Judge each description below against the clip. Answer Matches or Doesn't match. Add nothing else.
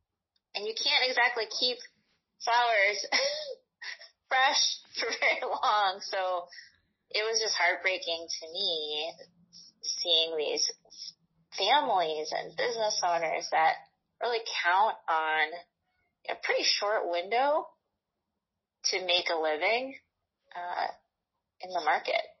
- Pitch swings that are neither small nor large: Doesn't match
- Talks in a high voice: Matches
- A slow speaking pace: Matches